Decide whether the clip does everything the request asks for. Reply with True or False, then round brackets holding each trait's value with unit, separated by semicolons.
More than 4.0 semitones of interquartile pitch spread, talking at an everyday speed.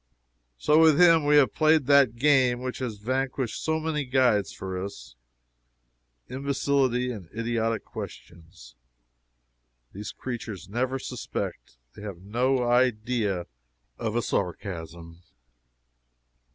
False (5.0 semitones; 110 wpm)